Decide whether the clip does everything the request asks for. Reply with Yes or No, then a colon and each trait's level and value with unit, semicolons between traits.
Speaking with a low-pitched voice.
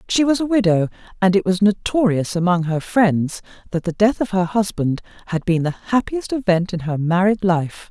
No: high, 190 Hz